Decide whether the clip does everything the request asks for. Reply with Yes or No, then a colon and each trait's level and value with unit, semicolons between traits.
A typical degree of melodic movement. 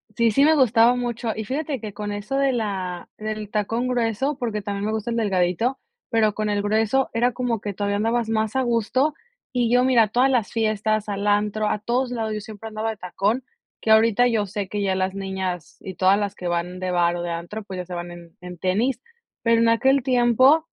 Yes: average, 3.2 semitones